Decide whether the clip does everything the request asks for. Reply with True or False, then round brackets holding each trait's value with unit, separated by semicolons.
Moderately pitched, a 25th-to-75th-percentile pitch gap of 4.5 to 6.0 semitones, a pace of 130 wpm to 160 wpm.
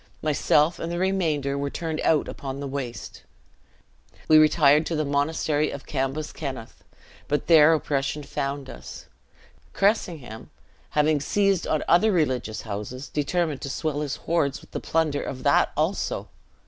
False (150 Hz; 2.7 semitones; 145 wpm)